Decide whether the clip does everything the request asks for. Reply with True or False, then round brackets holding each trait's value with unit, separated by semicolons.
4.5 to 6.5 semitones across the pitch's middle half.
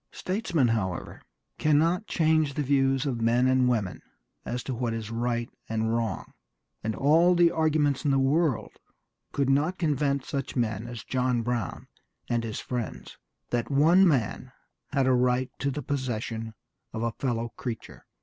False (3.9 semitones)